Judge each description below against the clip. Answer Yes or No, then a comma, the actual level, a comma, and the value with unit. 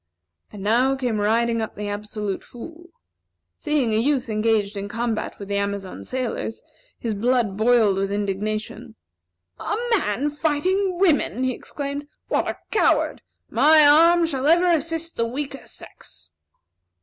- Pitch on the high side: Yes, high, 240 Hz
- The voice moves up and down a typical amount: No, wide, 5.8 semitones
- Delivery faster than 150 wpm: No, average, 140 wpm